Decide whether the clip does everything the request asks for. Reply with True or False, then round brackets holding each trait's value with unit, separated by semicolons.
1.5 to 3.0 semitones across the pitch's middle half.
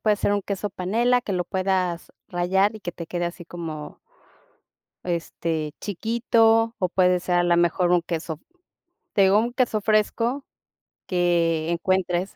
False (3.4 semitones)